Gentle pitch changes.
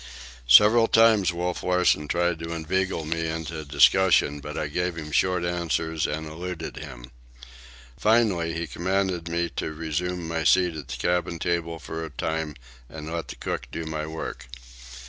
Yes: narrow, 2.2 semitones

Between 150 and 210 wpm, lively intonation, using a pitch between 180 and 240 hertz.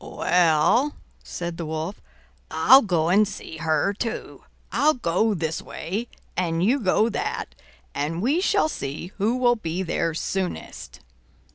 No: average, 140 wpm; wide, 6.4 semitones; medium, 185 Hz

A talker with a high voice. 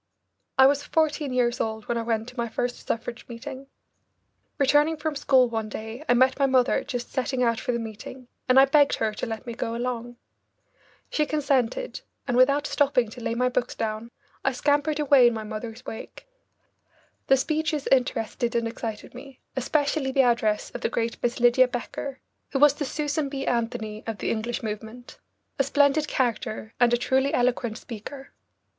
Yes: very high, 250 Hz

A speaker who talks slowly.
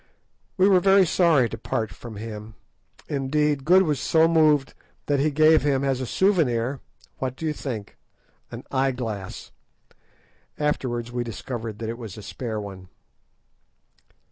No: average, 145 wpm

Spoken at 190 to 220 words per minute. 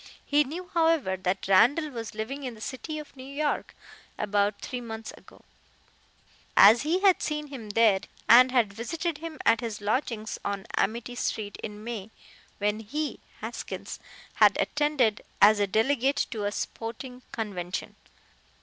No: average, 150 wpm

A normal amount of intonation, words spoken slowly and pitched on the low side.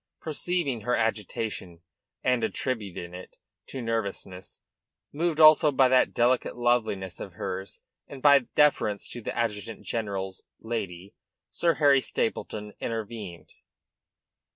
Yes: average, 4.8 semitones; slow, 115 wpm; low, 115 Hz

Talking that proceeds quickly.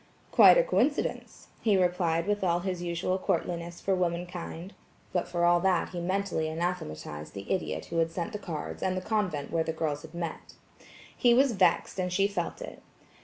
No: average, 185 wpm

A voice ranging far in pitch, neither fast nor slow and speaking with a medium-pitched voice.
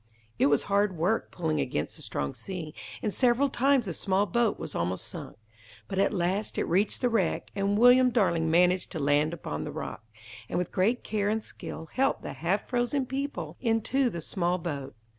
No: wide, 6.2 semitones; average, 195 wpm; high, 195 Hz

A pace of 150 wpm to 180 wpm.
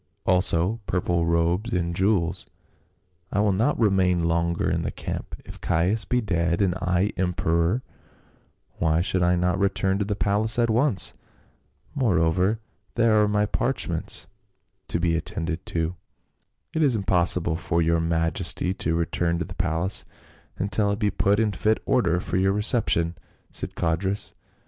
Yes: average, 155 wpm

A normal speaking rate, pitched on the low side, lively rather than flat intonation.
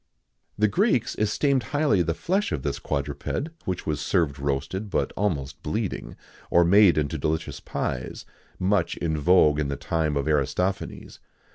Yes: average, 160 wpm; very low, 85 Hz; wide, 5.9 semitones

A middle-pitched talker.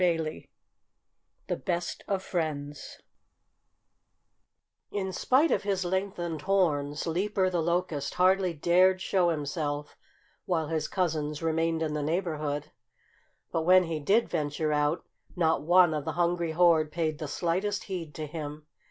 Yes: medium, 165 Hz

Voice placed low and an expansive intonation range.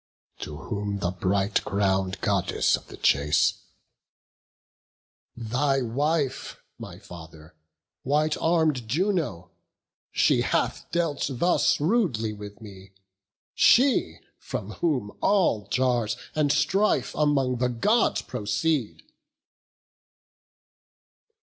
Yes: low, 120 Hz; wide, 7.4 semitones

